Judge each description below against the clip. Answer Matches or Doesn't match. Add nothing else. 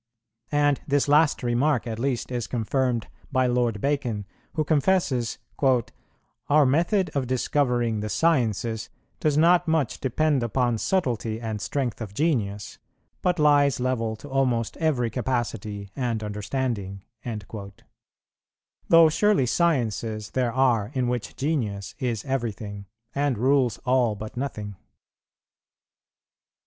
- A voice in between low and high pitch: Doesn't match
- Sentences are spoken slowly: Matches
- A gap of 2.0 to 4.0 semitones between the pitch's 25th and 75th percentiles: Doesn't match